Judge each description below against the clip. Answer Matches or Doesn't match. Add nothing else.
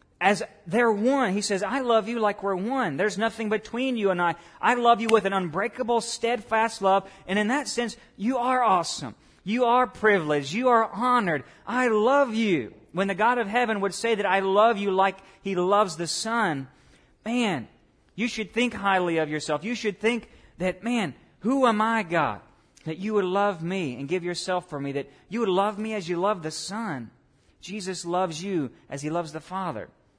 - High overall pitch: Matches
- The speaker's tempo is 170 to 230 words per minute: Matches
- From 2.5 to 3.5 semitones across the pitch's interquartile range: Doesn't match